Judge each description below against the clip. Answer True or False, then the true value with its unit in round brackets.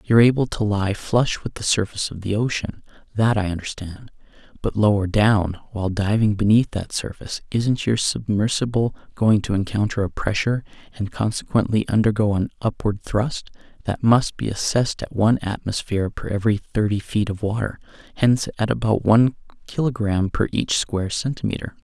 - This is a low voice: True (105 Hz)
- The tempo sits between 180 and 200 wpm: False (160 wpm)